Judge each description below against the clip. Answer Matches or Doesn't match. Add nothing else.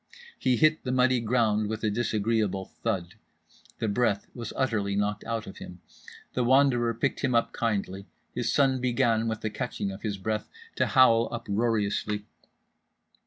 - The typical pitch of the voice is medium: Doesn't match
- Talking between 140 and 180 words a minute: Matches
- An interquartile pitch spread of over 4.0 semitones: Doesn't match